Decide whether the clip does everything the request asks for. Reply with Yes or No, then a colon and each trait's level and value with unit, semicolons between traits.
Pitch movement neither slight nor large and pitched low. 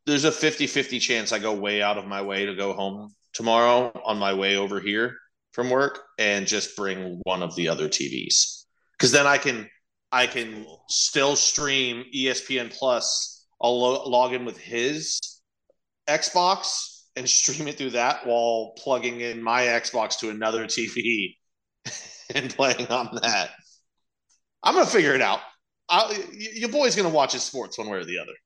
Yes: average, 4.2 semitones; low, 120 Hz